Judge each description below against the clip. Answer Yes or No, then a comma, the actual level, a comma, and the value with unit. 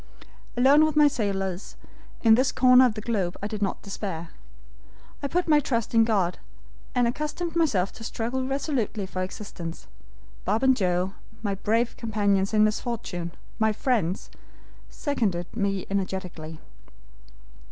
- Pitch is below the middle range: No, high, 215 Hz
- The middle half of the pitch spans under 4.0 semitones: No, average, 4.8 semitones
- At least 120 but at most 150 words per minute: Yes, average, 140 wpm